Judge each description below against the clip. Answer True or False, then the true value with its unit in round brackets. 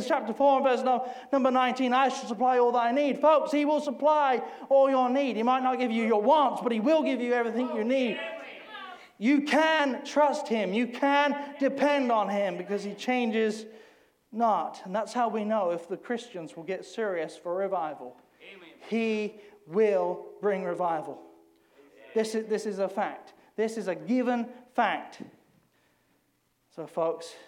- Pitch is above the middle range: True (240 Hz)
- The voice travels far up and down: False (4.5 semitones)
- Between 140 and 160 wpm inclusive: False (170 wpm)